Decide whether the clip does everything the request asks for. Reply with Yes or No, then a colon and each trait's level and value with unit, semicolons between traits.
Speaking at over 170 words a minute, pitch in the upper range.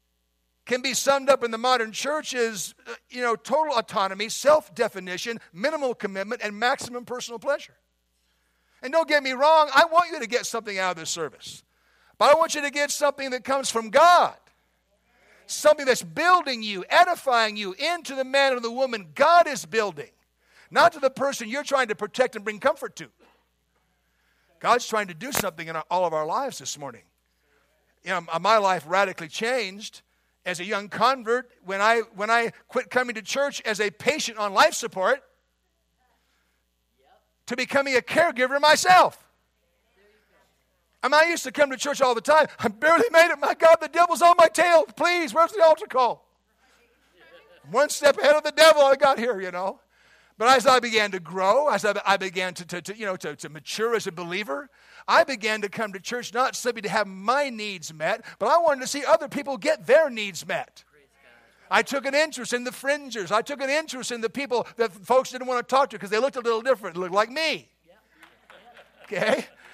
Yes: average, 200 wpm; high, 245 Hz